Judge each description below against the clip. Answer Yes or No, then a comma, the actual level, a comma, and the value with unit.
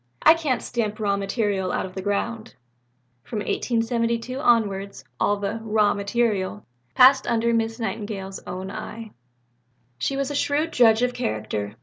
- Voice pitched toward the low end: No, high, 225 Hz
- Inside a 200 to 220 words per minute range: No, average, 140 wpm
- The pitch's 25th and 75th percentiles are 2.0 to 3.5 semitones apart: Yes, average, 3.2 semitones